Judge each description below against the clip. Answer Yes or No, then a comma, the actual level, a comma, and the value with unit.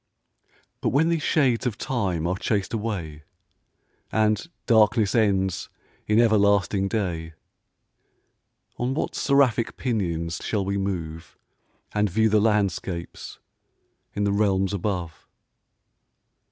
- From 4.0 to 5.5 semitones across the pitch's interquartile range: No, average, 3.2 semitones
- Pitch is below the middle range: Yes, low, 100 Hz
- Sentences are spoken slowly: Yes, slow, 110 wpm